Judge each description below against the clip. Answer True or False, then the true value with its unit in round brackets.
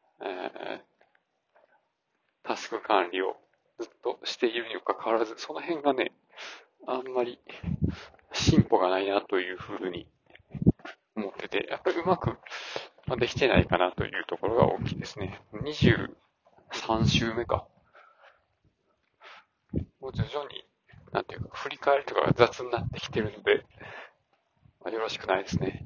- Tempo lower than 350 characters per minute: True (260 characters per minute)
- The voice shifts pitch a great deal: True (6.6 semitones)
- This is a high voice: False (130 Hz)